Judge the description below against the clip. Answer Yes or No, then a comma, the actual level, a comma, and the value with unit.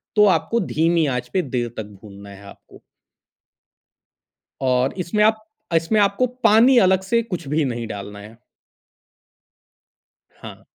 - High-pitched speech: No, medium, 160 Hz